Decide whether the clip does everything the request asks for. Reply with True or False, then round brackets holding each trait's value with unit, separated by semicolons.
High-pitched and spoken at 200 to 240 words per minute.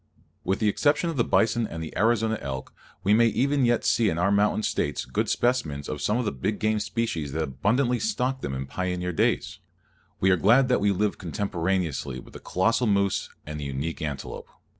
False (100 Hz; 205 wpm)